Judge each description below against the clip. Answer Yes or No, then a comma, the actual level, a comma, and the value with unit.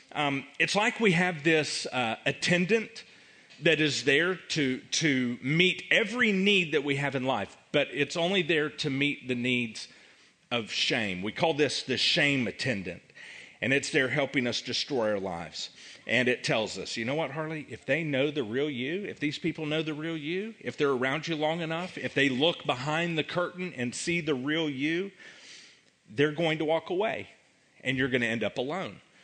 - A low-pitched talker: No, medium, 155 Hz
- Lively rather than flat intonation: No, average, 3.7 semitones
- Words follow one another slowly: No, average, 195 wpm